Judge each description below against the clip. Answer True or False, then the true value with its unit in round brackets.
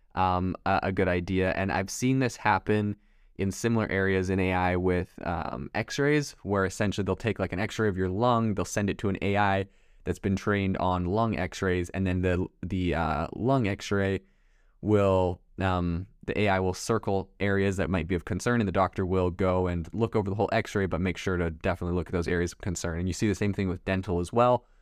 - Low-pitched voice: True (95 Hz)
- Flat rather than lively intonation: True (2.3 semitones)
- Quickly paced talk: True (220 wpm)